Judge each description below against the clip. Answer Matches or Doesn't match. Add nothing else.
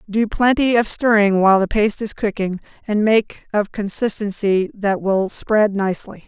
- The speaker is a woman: Matches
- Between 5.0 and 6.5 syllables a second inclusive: Doesn't match